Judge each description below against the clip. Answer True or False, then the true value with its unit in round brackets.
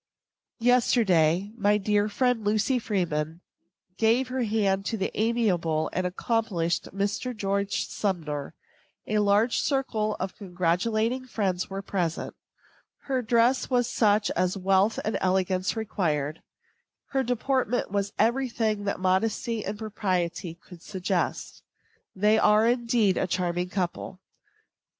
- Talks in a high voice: True (205 Hz)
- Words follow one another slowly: True (120 wpm)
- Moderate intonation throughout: True (3.7 semitones)